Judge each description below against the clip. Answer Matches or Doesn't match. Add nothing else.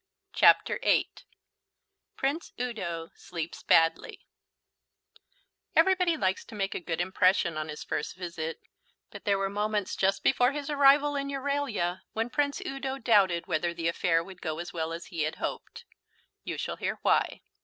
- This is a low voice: Doesn't match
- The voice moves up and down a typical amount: Doesn't match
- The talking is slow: Doesn't match